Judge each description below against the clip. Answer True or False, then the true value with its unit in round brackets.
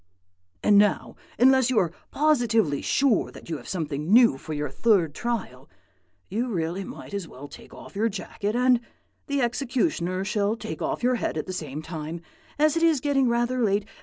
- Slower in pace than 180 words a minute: False (185 wpm)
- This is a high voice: True (210 Hz)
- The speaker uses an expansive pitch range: True (6.7 semitones)